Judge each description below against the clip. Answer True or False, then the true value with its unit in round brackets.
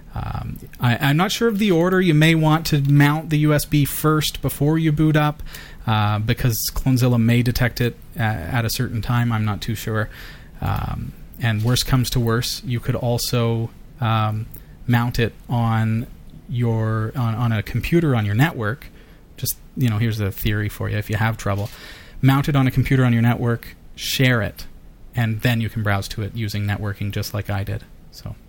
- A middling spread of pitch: True (3.6 semitones)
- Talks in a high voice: False (120 Hz)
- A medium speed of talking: True (195 wpm)